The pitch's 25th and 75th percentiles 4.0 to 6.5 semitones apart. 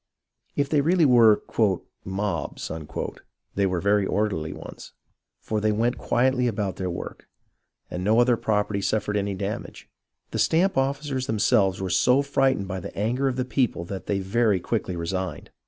Yes: average, 4.6 semitones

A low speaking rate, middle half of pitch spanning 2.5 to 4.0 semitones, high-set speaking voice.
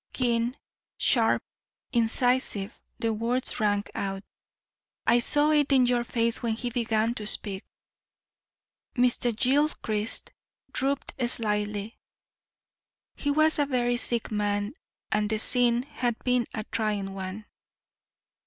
Yes: slow, 115 wpm; average, 2.9 semitones; high, 235 Hz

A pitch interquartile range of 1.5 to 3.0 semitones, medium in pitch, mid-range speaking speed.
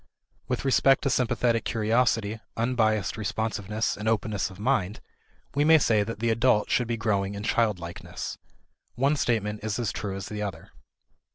No: narrow, 2.6 semitones; low, 110 Hz; average, 160 wpm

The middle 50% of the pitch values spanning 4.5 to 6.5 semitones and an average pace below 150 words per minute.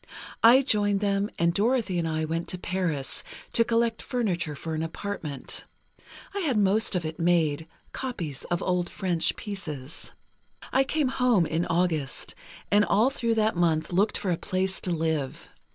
No: average, 4.9 semitones; average, 165 wpm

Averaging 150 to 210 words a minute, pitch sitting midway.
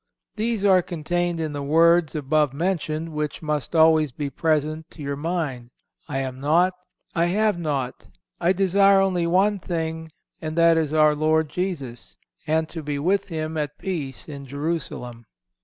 Yes: average, 160 wpm; medium, 160 Hz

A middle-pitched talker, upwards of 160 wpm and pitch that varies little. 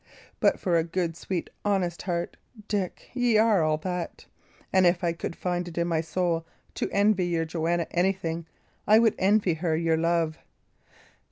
Yes: medium, 175 Hz; average, 175 wpm; narrow, 2.3 semitones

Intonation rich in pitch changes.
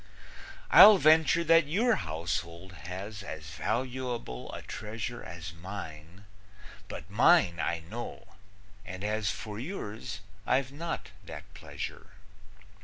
Yes: wide, 7.1 semitones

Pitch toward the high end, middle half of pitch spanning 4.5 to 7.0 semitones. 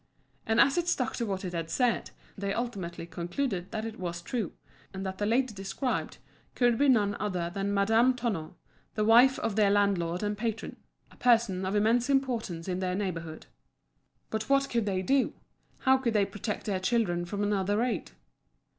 No: high, 210 Hz; average, 4.1 semitones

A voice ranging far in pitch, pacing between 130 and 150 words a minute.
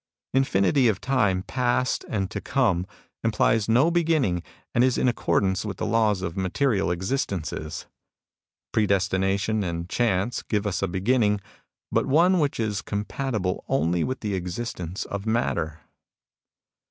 No: average, 4.7 semitones; average, 140 wpm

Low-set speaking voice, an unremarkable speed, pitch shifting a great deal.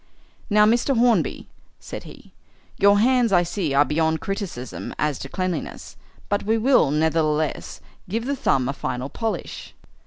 No: medium, 185 Hz; average, 150 wpm; wide, 6.8 semitones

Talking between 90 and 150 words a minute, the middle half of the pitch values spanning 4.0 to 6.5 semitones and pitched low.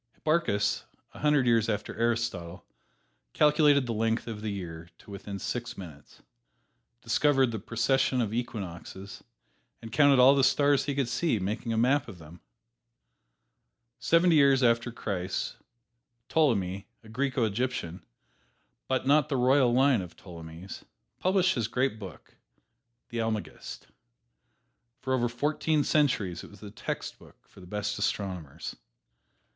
Yes: average, 140 wpm; average, 5.2 semitones; low, 115 Hz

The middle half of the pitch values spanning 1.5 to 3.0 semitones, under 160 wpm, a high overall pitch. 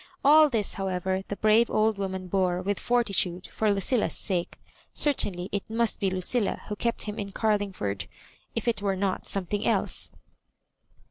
No: average, 2.7 semitones; average, 170 wpm; high, 200 Hz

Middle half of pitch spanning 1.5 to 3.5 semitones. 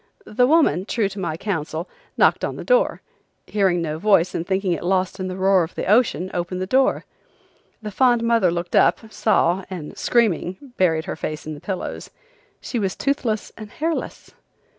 No: average, 4.2 semitones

